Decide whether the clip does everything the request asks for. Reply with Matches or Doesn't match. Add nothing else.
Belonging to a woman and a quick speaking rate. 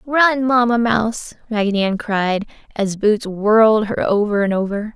Doesn't match